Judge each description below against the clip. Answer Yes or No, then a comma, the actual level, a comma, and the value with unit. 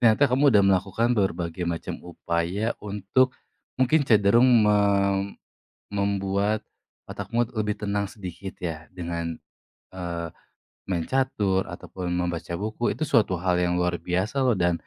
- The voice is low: Yes, very low, 95 Hz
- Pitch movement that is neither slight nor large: Yes, average, 3.8 semitones